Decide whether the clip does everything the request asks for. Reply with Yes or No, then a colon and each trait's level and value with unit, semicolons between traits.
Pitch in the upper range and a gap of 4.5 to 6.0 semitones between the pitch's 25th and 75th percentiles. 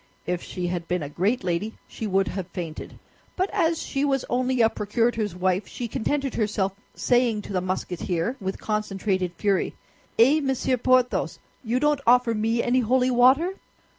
Yes: high, 225 Hz; average, 5.2 semitones